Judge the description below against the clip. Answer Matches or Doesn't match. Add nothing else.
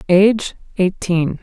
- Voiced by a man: Doesn't match